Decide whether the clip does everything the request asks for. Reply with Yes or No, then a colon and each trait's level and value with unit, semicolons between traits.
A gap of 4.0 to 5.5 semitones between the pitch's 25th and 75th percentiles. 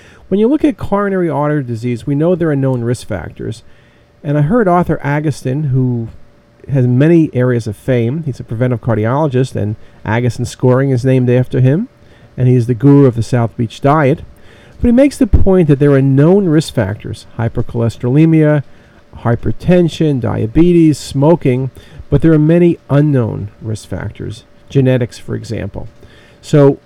Yes: average, 4.4 semitones